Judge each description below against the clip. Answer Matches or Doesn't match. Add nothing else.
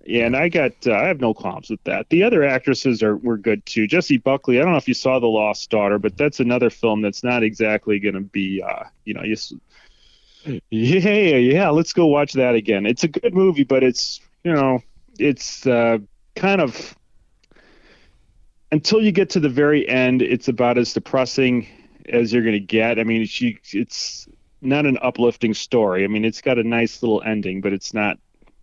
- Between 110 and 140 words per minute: Doesn't match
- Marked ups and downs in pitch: Doesn't match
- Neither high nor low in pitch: Doesn't match